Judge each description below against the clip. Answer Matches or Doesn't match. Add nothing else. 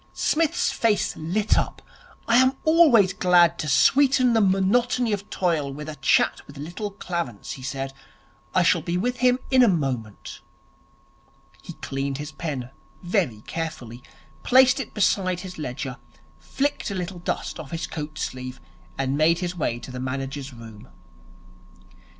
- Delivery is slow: Doesn't match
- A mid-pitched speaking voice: Matches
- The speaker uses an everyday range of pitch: Doesn't match